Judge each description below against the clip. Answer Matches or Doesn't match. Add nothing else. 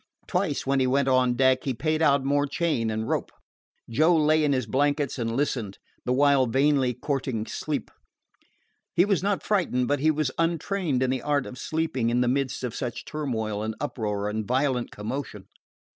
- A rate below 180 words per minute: Doesn't match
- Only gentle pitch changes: Doesn't match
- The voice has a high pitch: Doesn't match